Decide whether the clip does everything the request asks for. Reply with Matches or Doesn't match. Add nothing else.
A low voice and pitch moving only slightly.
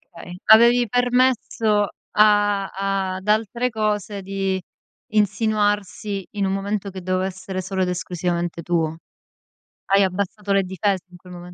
Doesn't match